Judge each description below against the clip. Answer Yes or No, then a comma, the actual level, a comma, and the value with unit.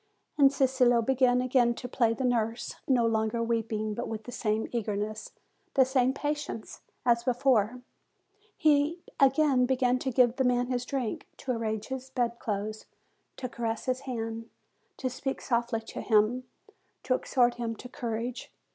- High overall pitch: Yes, high, 245 Hz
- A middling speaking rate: Yes, average, 155 wpm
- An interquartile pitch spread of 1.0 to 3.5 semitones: Yes, narrow, 2.4 semitones